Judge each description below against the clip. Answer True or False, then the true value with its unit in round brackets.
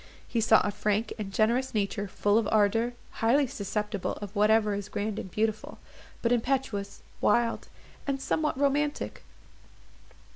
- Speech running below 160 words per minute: True (140 wpm)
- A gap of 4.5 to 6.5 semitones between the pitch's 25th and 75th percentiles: False (2.8 semitones)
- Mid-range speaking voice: False (220 Hz)